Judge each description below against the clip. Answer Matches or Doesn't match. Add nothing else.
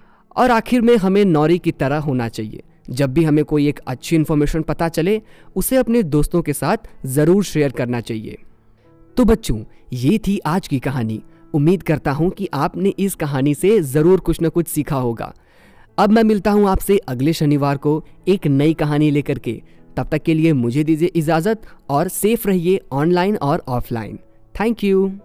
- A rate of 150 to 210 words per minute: Matches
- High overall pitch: Doesn't match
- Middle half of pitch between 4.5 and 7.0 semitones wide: Matches